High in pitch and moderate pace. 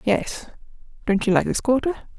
Yes: high, 235 Hz; average, 165 wpm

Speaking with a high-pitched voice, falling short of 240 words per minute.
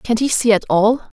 No: high, 225 Hz; fast, 250 wpm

